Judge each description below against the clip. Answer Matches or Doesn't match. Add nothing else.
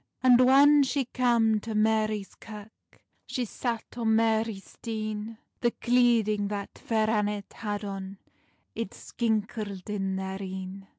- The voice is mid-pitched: Doesn't match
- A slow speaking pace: Matches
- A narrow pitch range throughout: Matches